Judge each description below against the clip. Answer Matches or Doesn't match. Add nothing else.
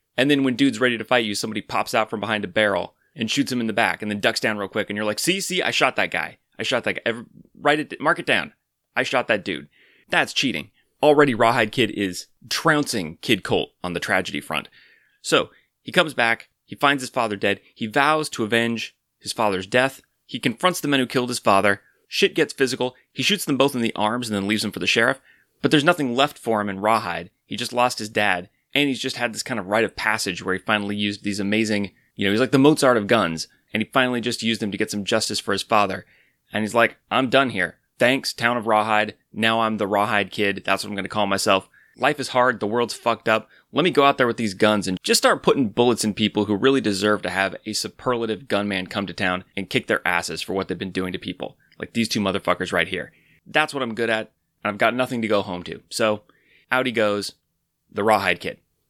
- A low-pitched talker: Matches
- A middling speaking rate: Doesn't match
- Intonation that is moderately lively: Matches